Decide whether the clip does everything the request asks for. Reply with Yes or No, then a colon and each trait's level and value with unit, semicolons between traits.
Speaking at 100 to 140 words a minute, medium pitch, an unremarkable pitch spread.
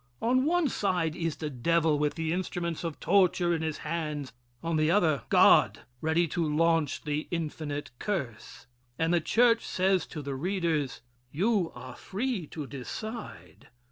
No: average, 155 wpm; medium, 165 Hz; average, 3.6 semitones